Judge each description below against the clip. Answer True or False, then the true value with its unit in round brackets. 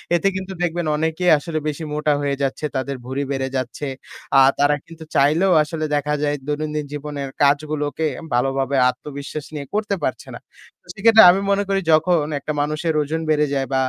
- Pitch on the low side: False (150 Hz)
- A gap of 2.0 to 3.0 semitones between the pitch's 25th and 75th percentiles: True (2.4 semitones)